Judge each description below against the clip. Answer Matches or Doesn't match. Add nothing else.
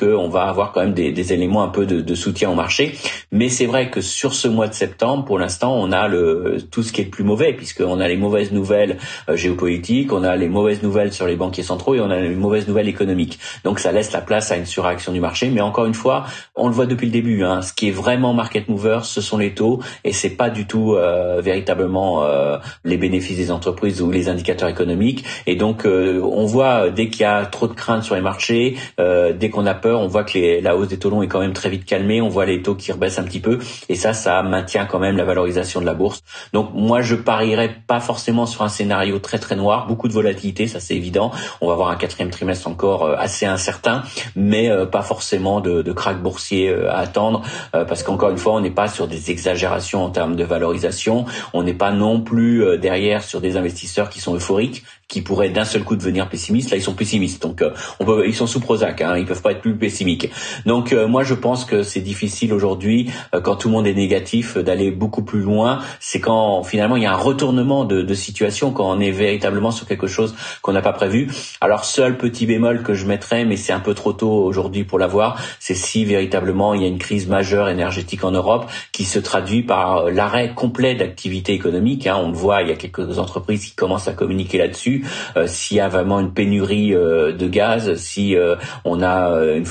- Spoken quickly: Matches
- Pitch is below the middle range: Matches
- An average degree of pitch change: Matches